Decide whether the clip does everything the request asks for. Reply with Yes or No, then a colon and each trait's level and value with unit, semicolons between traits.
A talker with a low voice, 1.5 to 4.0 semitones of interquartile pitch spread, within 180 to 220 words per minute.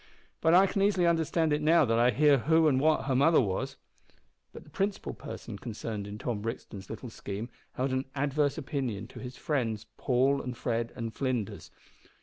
No: low, 130 Hz; average, 4.9 semitones; average, 185 wpm